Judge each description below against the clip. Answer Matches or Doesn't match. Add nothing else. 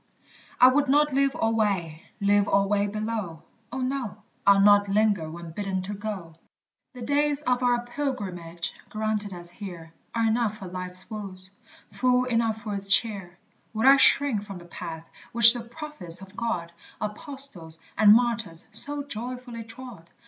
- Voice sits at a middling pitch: Doesn't match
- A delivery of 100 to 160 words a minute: Matches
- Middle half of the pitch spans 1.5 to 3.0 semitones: Doesn't match